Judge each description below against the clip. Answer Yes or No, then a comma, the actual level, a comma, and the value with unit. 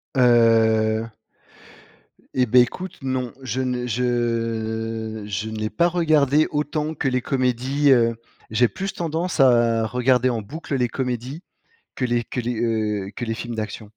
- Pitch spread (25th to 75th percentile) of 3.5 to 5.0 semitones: No, average, 2.9 semitones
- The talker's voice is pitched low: Yes, low, 120 Hz